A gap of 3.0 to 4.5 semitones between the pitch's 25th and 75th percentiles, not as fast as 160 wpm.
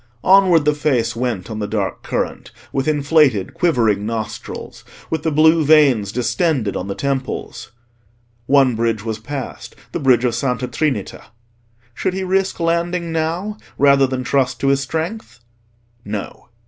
No: wide, 5.6 semitones; average, 145 wpm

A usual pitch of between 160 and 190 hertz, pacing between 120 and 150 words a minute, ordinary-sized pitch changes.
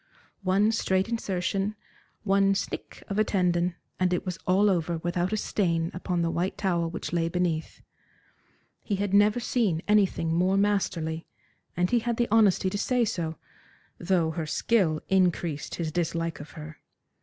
No: medium, 185 Hz; average, 160 wpm; average, 3.2 semitones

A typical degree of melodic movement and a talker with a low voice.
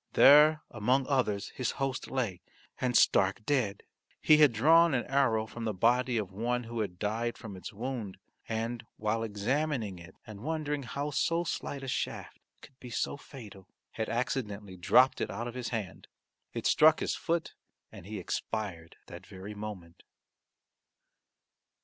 Yes: average, 4.5 semitones; low, 115 Hz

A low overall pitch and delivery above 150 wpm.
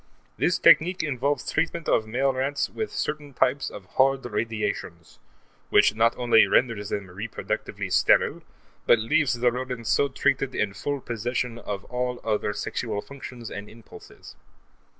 No: low, 125 Hz; average, 145 wpm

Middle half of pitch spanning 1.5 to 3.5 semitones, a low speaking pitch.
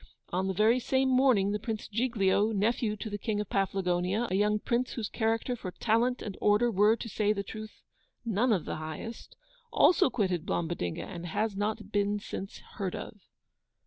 No: average, 2.8 semitones; high, 210 Hz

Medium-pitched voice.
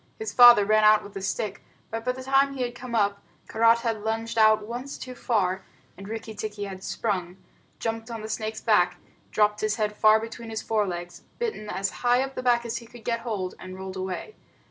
No: high, 220 Hz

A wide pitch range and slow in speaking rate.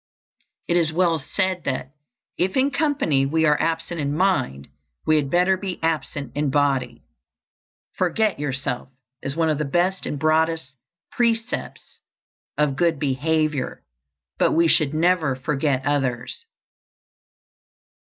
No: average, 4.1 semitones; slow, 130 wpm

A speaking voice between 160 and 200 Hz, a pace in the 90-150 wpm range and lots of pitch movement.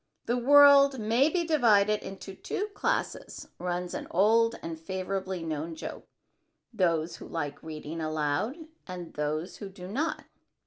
Yes: high, 190 Hz; average, 140 wpm; wide, 6.4 semitones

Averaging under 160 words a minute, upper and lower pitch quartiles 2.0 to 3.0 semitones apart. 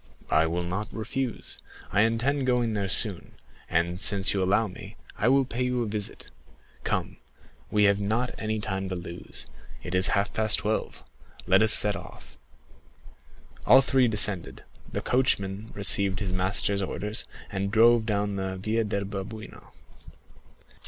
Yes: average, 150 wpm; average, 2.7 semitones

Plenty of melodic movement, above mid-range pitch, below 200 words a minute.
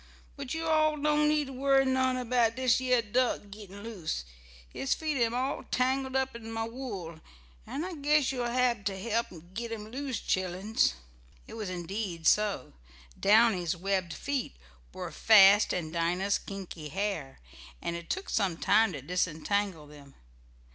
Yes: wide, 5.9 semitones; high, 220 Hz; average, 160 wpm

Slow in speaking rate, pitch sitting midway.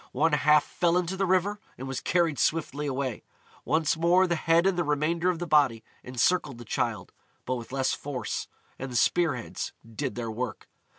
No: average, 190 wpm; medium, 150 Hz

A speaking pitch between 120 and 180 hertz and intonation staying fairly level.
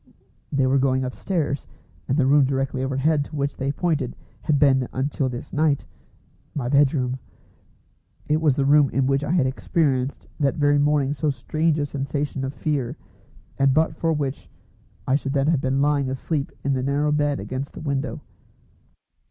Yes: medium, 140 Hz; narrow, 1.9 semitones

